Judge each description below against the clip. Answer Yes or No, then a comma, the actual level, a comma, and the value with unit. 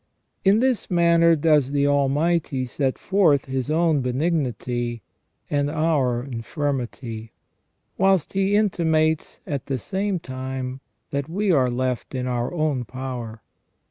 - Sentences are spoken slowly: Yes, slow, 125 wpm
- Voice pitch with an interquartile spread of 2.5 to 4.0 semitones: No, average, 4.6 semitones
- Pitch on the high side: No, medium, 140 Hz